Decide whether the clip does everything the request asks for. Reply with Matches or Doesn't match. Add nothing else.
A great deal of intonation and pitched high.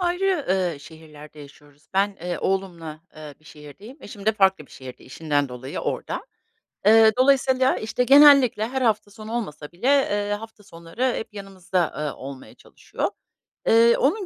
Matches